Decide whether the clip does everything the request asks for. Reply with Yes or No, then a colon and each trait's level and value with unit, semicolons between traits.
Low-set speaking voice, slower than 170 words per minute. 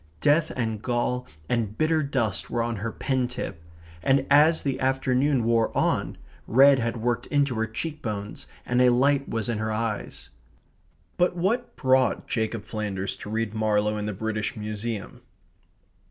Yes: low, 120 Hz; average, 160 wpm